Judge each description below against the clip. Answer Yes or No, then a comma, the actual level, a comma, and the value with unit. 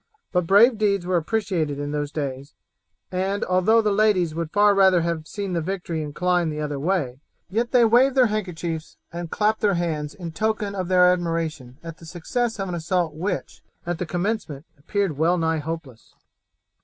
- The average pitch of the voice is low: No, medium, 175 Hz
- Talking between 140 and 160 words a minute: No, average, 180 wpm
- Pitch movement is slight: No, average, 4.1 semitones